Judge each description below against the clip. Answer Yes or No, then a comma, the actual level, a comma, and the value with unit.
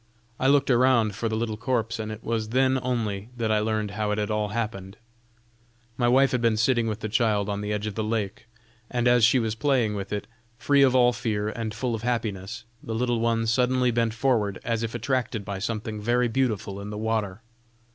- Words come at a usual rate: No, fast, 215 wpm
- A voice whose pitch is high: No, low, 115 Hz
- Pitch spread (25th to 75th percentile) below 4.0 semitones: Yes, narrow, 2.4 semitones